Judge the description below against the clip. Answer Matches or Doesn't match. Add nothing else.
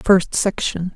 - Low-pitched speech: Doesn't match